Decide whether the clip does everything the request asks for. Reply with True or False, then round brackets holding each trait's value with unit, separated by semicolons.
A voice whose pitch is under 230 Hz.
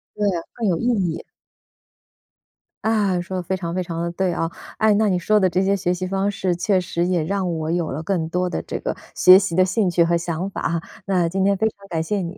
True (185 Hz)